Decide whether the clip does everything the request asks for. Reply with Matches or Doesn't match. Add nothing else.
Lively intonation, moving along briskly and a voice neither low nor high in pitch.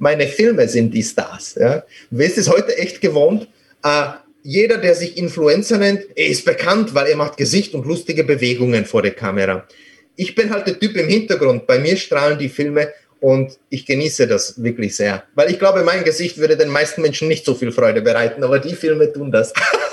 Matches